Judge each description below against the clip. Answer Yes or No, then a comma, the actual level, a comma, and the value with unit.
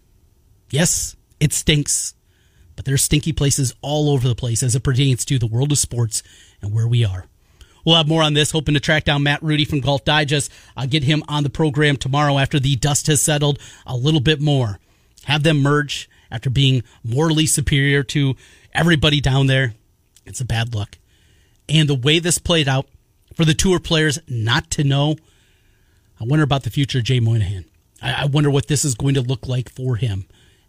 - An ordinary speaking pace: Yes, average, 195 wpm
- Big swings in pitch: No, average, 4.8 semitones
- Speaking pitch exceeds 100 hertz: Yes, low, 135 Hz